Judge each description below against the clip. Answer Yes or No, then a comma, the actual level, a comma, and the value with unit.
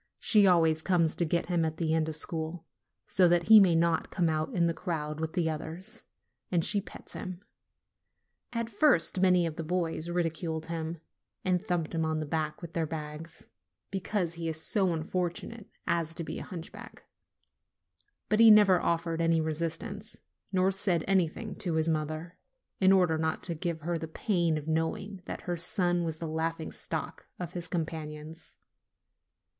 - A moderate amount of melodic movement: No, narrow, 2.2 semitones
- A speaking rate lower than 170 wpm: No, average, 175 wpm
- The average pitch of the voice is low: No, medium, 170 Hz